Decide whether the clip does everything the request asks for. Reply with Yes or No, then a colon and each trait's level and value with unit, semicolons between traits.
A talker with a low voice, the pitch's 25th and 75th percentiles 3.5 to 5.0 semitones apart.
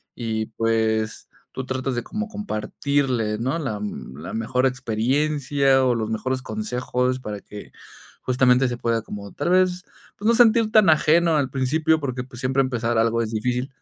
Yes: low, 130 Hz; average, 4.2 semitones